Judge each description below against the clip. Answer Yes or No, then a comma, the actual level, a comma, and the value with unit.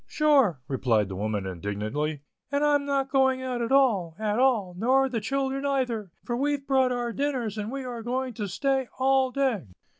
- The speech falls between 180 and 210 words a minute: Yes, average, 185 wpm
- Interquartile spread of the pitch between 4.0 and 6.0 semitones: Yes, wide, 5.4 semitones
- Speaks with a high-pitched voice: Yes, very high, 250 Hz